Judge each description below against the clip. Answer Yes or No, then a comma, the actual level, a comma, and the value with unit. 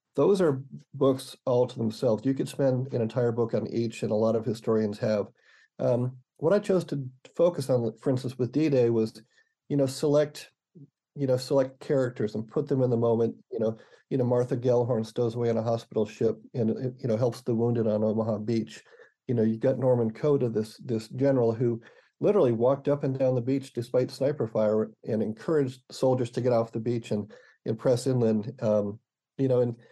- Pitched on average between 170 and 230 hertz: No, low, 125 Hz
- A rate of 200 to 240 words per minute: Yes, fast, 205 wpm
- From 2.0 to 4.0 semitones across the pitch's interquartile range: Yes, average, 2.9 semitones